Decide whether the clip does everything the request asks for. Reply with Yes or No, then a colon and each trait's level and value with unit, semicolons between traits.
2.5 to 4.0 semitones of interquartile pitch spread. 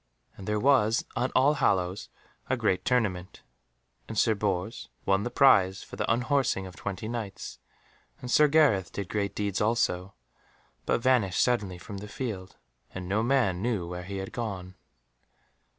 No: average, 4.4 semitones